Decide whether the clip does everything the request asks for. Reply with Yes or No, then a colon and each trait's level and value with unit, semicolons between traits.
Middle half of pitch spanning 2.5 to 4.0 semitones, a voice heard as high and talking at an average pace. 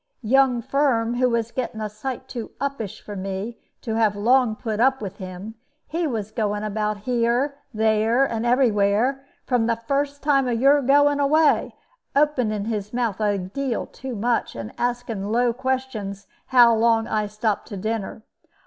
Yes: average, 3.6 semitones; high, 230 Hz; average, 170 wpm